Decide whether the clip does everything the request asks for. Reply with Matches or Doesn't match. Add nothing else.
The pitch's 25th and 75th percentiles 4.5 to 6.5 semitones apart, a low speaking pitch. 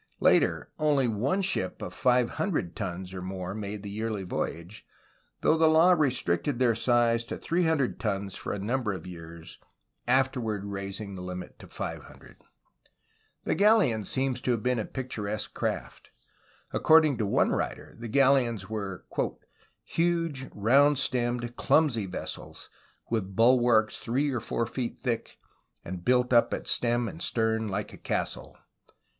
Matches